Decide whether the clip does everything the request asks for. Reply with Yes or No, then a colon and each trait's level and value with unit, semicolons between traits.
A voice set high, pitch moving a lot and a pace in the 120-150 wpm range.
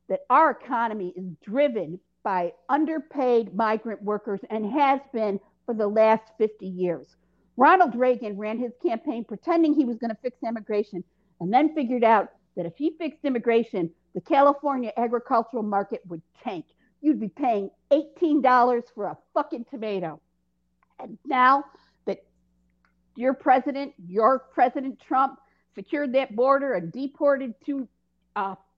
Yes: high, 235 Hz; wide, 5.7 semitones; average, 140 wpm